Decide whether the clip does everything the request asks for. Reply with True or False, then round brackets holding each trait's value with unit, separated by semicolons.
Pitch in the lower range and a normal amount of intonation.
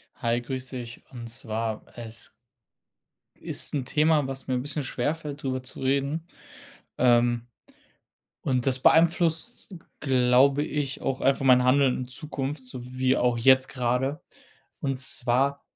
False (130 Hz; 2.1 semitones)